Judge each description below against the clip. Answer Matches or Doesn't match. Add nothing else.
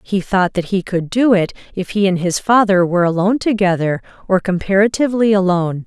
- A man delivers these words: Doesn't match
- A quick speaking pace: Doesn't match